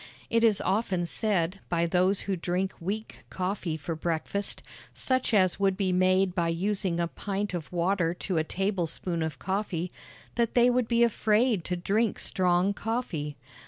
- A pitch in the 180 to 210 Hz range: Yes, medium, 185 Hz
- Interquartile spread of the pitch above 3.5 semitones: No, average, 3.2 semitones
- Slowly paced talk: No, average, 160 wpm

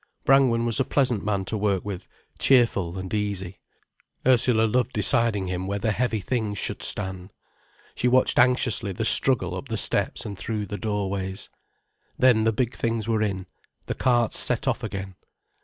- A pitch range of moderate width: Yes, average, 3.6 semitones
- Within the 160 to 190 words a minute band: Yes, average, 170 wpm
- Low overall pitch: Yes, low, 105 Hz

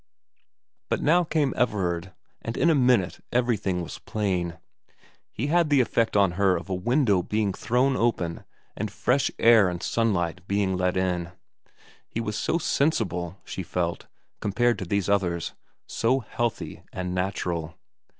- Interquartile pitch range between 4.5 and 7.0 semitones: Yes, average, 5.0 semitones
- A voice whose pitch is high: No, low, 100 Hz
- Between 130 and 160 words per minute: Yes, average, 150 wpm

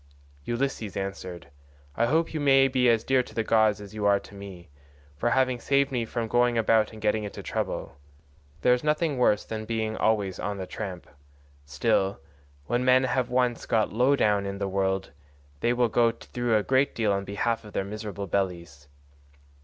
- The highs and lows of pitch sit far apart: No, average, 3.8 semitones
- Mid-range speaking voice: No, low, 110 Hz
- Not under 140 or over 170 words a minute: No, average, 190 wpm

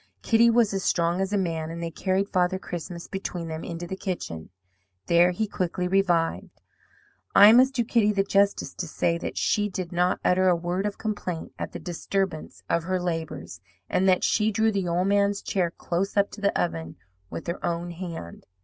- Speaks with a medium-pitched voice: Yes, medium, 180 Hz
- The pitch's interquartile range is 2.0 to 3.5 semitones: Yes, average, 2.8 semitones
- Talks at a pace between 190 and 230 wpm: Yes, average, 195 wpm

